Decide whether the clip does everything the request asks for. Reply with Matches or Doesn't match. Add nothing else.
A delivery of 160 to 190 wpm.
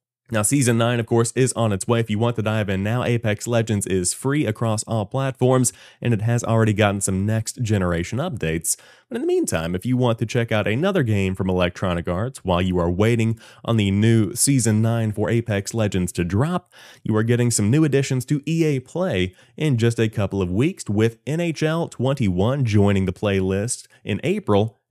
Doesn't match